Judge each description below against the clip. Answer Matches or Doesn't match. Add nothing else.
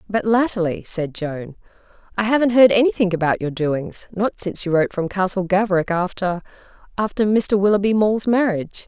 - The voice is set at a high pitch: Matches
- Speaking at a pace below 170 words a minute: Matches